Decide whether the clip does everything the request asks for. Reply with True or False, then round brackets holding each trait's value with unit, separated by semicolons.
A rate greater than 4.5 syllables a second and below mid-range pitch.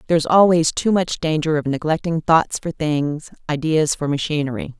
False (5.2 syllables/s; 155 Hz)